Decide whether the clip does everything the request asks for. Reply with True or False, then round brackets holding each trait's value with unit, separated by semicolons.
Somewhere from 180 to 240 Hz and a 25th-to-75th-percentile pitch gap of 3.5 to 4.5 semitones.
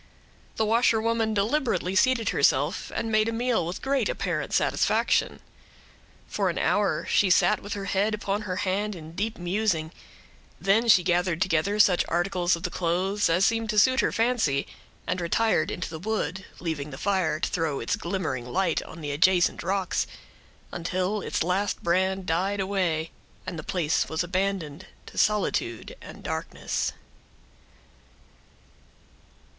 True (190 Hz; 3.8 semitones)